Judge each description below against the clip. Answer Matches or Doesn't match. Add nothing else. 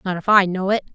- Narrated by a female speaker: Matches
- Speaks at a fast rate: Matches